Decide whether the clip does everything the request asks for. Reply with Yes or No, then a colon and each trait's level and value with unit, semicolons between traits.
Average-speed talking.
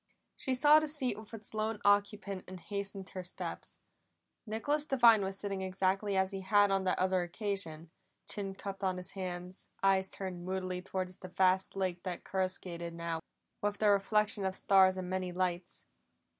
Yes: average, 170 wpm